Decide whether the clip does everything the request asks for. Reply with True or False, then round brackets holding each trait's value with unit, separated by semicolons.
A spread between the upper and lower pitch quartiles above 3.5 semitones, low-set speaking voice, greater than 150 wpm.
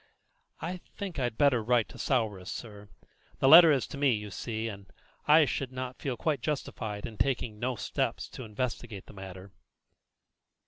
True (4.6 semitones; 120 Hz; 170 wpm)